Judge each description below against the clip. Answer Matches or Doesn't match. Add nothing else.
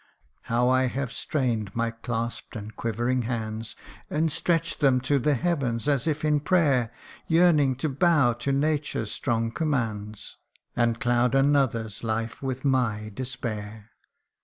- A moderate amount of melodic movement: Matches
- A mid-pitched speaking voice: Doesn't match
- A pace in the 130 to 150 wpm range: Matches